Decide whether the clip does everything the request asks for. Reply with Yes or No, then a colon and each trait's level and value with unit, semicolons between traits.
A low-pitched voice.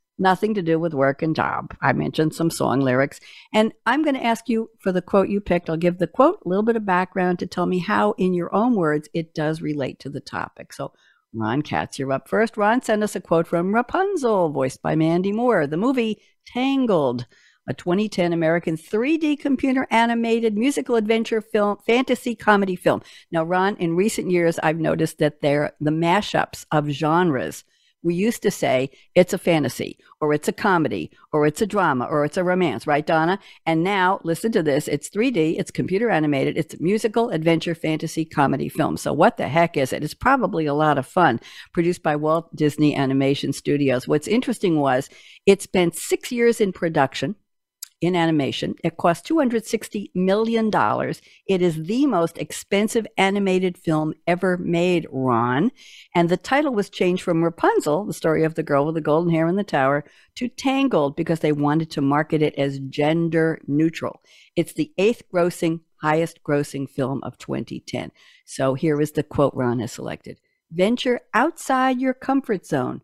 No: medium, 170 Hz